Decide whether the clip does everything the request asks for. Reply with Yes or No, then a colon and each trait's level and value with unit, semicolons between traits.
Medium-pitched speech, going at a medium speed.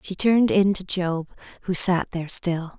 Yes: medium, 180 Hz; average, 195 wpm